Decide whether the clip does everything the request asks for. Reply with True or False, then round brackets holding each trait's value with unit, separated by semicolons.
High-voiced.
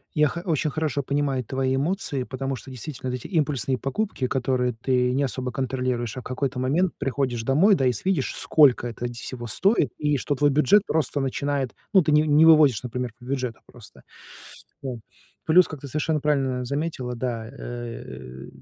False (135 Hz)